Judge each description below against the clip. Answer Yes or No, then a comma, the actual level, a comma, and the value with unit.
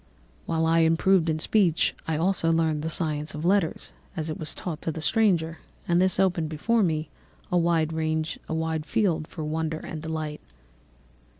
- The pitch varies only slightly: Yes, narrow, 1.5 semitones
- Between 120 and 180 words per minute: Yes, average, 165 wpm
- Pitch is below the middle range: No, medium, 160 Hz